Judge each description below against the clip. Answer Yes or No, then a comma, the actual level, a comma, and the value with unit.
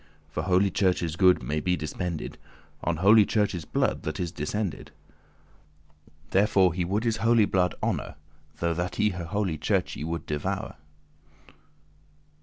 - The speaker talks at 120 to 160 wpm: Yes, average, 140 wpm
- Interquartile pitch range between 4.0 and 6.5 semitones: No, average, 3.2 semitones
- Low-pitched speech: Yes, very low, 90 Hz